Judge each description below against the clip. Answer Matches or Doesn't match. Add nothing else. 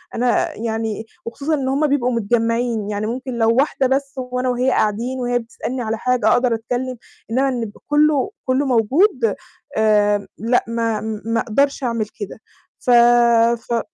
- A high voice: Matches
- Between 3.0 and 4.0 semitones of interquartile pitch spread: Doesn't match